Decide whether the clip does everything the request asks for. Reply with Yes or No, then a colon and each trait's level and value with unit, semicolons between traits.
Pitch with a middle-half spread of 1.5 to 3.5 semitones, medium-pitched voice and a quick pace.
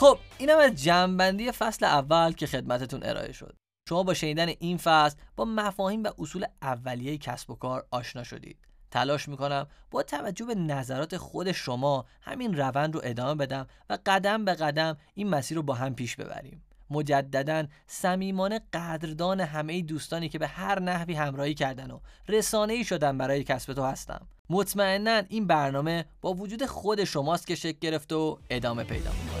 No: average, 5.3 semitones; medium, 160 Hz; fast, 170 wpm